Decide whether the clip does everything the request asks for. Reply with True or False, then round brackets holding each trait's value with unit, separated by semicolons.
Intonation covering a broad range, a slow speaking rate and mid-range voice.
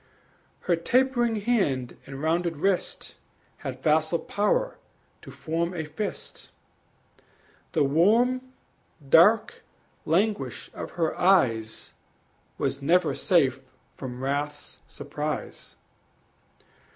True (6.2 semitones; 90 wpm; 165 Hz)